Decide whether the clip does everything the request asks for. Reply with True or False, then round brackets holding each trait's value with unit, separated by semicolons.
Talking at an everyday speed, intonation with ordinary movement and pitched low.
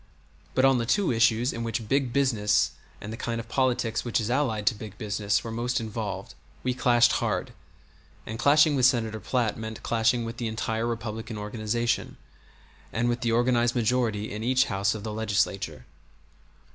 False (175 wpm; 2.1 semitones; 115 Hz)